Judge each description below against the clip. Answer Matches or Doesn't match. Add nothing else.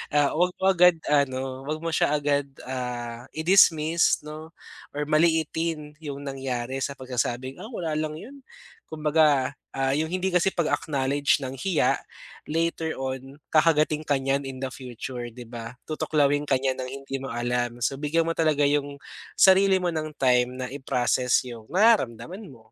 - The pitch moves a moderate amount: Matches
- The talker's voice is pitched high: Doesn't match